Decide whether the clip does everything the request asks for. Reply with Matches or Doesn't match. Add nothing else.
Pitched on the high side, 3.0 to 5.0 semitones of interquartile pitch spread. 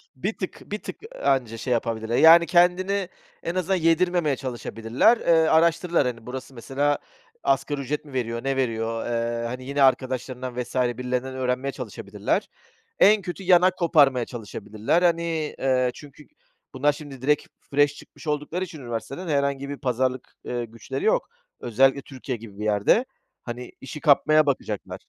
Doesn't match